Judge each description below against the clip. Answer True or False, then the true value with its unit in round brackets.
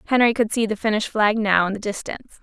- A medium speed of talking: False (250 wpm)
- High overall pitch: True (215 Hz)